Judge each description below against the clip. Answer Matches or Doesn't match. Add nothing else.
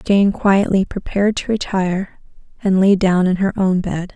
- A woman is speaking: Matches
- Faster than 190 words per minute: Doesn't match